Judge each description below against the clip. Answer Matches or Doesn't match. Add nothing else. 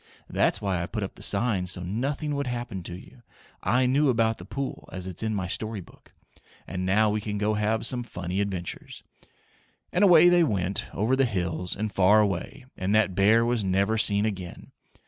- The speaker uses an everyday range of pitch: Matches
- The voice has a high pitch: Doesn't match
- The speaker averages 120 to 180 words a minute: Doesn't match